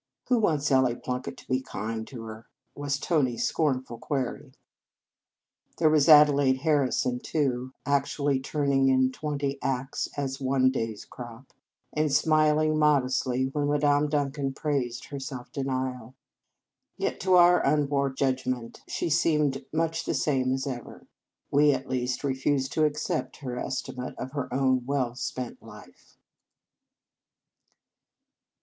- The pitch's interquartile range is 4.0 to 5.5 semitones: No, narrow, 2.4 semitones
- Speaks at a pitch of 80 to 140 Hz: Yes, low, 135 Hz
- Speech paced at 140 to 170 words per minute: Yes, average, 155 wpm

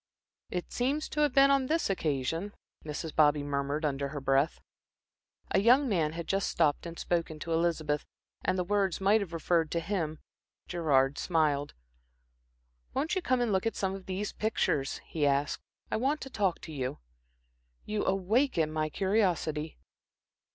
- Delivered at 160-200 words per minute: Yes, average, 165 wpm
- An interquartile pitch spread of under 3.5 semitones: No, wide, 5.4 semitones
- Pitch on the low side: No, medium, 170 Hz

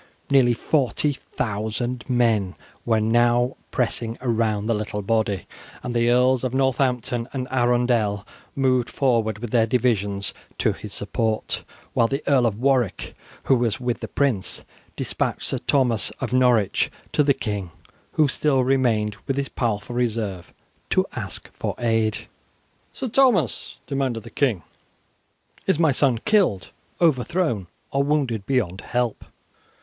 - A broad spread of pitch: No, average, 3.2 semitones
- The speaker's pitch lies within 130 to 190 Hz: No, low, 120 Hz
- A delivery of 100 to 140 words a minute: Yes, slow, 135 wpm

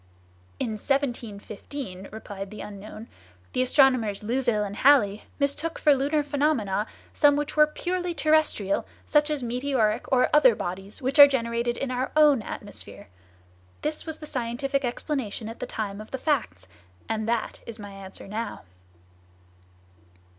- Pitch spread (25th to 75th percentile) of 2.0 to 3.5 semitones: No, average, 5.2 semitones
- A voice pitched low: No, high, 245 Hz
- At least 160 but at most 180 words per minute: No, average, 145 wpm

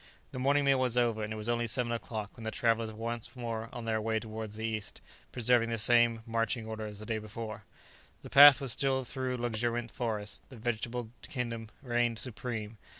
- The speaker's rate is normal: No, fast, 210 wpm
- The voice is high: No, low, 115 Hz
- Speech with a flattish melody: Yes, narrow, 1.7 semitones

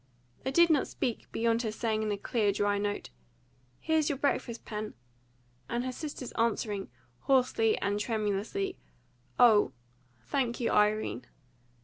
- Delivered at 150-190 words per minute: No, slow, 135 wpm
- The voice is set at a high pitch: Yes, high, 225 Hz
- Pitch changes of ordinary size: Yes, average, 3.5 semitones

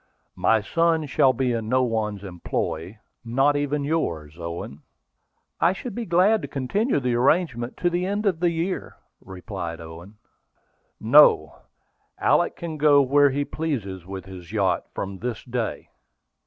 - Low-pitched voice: Yes, low, 125 Hz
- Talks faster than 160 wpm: No, average, 155 wpm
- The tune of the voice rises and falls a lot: Yes, wide, 8.6 semitones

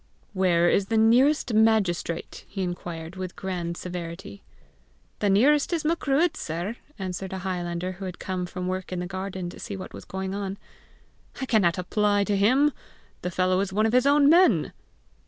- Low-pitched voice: No, high, 190 Hz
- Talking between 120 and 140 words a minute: No, average, 180 wpm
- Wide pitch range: No, average, 3.5 semitones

